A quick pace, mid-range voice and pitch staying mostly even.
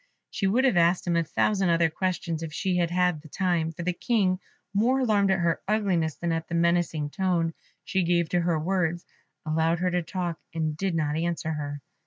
Yes: fast, 210 wpm; medium, 170 Hz; narrow, 2.3 semitones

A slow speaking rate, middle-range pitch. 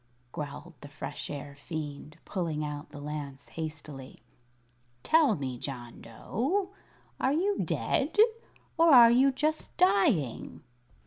Yes: slow, 120 wpm; medium, 155 Hz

